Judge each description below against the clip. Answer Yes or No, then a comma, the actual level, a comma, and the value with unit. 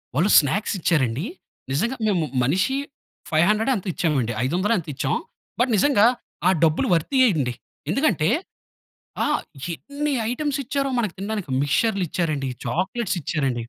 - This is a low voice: No, medium, 185 Hz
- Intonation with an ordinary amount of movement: No, wide, 7.5 semitones